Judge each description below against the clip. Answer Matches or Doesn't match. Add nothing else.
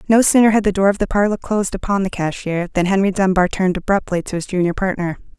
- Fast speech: Matches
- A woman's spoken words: Matches